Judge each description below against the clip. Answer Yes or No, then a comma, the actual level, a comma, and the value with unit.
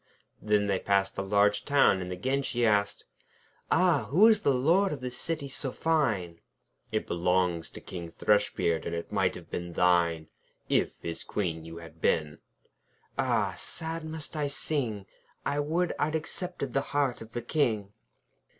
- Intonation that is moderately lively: No, wide, 8.4 semitones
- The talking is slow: No, average, 170 wpm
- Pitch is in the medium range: No, low, 110 Hz